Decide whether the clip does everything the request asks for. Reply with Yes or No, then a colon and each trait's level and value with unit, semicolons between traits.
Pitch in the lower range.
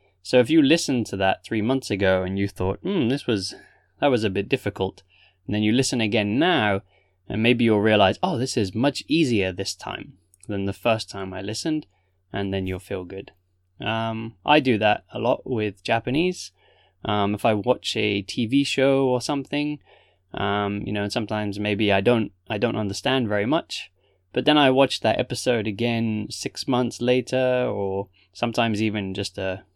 Yes: low, 105 Hz